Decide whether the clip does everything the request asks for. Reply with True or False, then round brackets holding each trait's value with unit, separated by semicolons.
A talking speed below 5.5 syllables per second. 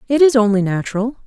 False (6.4 syllables/s)